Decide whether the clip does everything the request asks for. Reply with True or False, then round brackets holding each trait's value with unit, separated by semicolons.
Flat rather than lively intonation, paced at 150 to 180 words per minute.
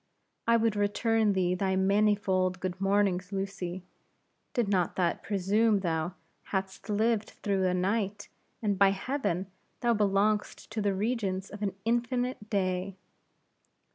False (2.1 semitones; 135 wpm)